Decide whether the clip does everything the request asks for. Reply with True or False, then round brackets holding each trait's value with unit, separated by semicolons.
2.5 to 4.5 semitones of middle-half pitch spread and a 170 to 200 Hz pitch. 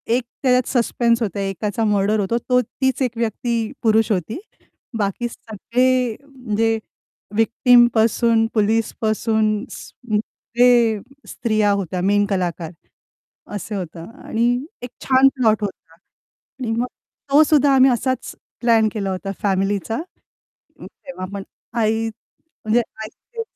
False (3.1 semitones; 225 Hz)